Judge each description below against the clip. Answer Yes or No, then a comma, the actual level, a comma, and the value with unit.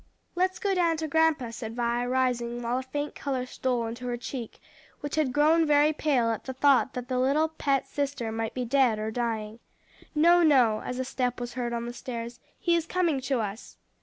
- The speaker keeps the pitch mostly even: No, average, 3.8 semitones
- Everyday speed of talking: No, fast, 210 wpm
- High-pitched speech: Yes, very high, 255 Hz